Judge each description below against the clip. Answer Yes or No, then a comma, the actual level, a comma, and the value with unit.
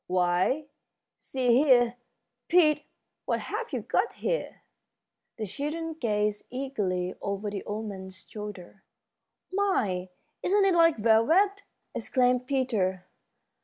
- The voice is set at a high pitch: Yes, high, 240 Hz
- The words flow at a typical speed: No, slow, 110 wpm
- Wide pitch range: Yes, wide, 7.5 semitones